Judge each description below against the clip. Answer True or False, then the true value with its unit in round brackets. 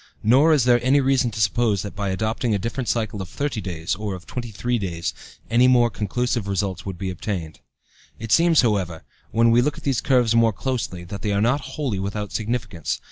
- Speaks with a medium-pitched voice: False (110 Hz)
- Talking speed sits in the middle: False (210 wpm)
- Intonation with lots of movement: False (4.0 semitones)